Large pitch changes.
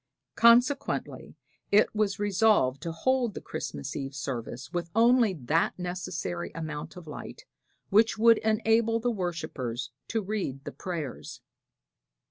Yes: wide, 7.6 semitones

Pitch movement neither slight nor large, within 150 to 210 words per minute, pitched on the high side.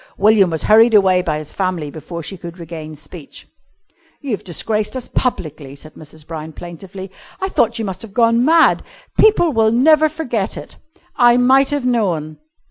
No: wide, 6.7 semitones; average, 170 wpm; high, 195 Hz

